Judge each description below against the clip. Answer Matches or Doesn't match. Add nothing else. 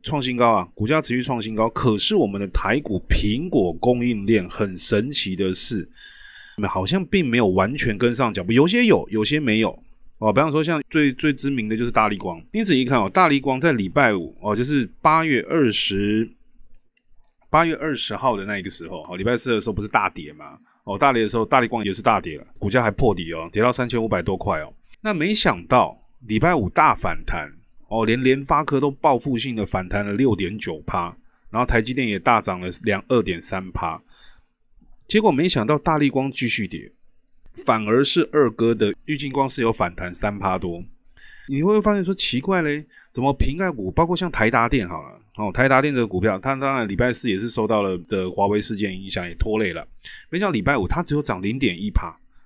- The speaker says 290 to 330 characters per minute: Matches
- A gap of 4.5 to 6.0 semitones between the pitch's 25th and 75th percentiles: Matches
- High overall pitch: Doesn't match